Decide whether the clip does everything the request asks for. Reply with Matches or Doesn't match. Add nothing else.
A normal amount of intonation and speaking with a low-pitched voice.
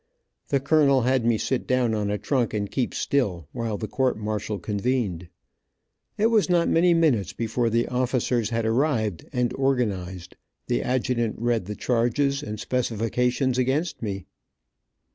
Matches